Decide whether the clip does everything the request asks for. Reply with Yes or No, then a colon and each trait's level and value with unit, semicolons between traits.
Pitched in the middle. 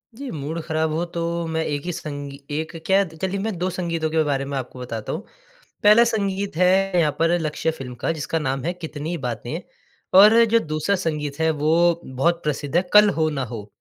Yes: medium, 160 Hz